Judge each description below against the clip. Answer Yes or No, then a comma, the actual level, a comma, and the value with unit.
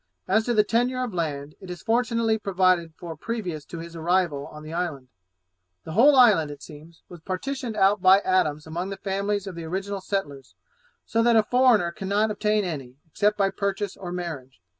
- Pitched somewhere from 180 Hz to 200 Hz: Yes, high, 190 Hz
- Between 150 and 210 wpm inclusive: Yes, average, 190 wpm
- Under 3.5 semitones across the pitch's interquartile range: No, average, 4.5 semitones